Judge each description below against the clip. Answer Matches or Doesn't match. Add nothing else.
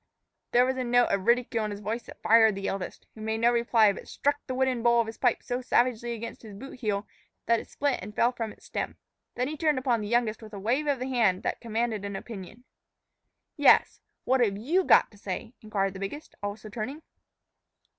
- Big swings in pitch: Doesn't match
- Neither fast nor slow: Doesn't match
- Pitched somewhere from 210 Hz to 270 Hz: Matches